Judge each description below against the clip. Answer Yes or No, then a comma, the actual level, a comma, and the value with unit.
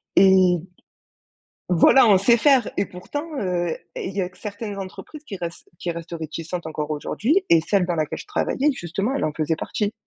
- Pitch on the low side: No, medium, 185 Hz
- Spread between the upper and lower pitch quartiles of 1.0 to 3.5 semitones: No, average, 4.1 semitones